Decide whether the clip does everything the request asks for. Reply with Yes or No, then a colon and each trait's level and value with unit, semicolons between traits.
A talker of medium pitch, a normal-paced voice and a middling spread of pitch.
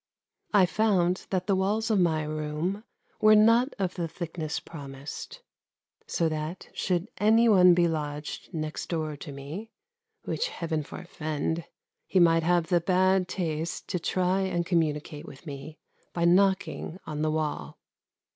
Yes: medium, 170 Hz; average, 145 wpm; average, 3.5 semitones